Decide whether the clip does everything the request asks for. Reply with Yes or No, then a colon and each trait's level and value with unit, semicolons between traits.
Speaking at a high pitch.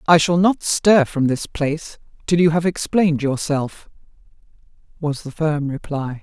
No: medium, 155 Hz